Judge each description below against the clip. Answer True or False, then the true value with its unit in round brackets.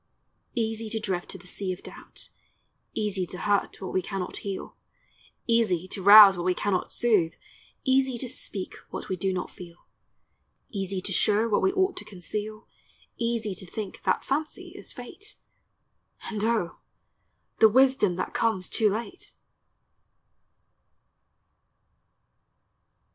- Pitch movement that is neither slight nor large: True (3.6 semitones)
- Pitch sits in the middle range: False (210 Hz)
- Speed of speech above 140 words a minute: False (135 wpm)